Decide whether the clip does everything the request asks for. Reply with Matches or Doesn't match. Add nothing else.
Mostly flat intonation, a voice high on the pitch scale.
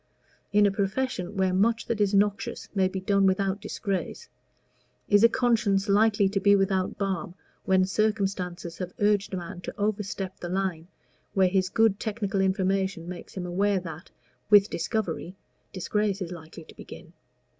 Matches